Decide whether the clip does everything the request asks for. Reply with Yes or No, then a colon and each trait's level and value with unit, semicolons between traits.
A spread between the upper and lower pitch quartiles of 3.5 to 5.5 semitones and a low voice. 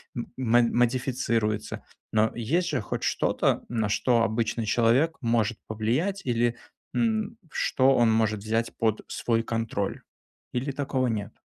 No: narrow, 2.6 semitones; low, 115 Hz